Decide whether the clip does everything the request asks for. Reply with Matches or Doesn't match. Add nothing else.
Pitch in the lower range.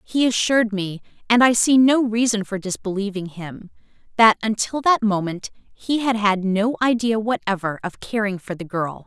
Doesn't match